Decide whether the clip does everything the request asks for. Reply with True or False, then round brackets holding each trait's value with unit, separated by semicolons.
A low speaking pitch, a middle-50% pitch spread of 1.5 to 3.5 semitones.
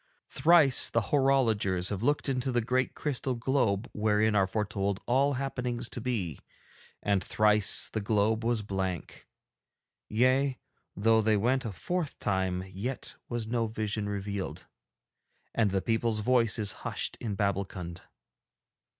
False (110 Hz; 4.0 semitones)